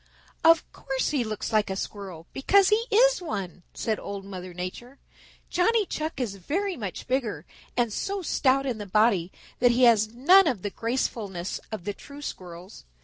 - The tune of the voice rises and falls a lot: Yes, wide, 7.1 semitones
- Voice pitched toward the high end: Yes, high, 235 Hz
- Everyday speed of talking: Yes, average, 175 wpm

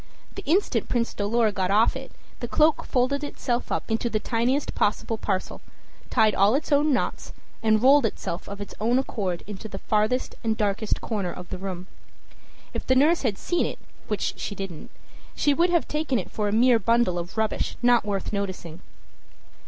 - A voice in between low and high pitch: No, high, 220 Hz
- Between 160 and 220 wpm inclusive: Yes, average, 185 wpm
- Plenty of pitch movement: No, average, 4.3 semitones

